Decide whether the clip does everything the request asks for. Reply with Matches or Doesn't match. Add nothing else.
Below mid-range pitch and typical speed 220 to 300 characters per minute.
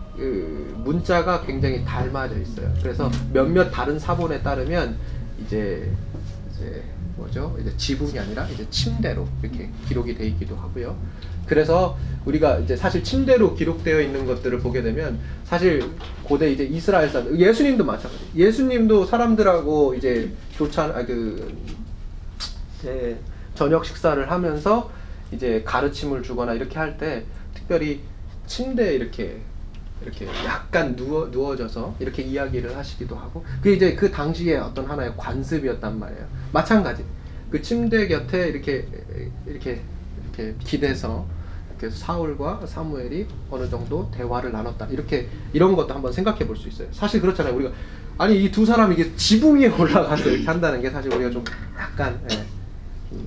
Doesn't match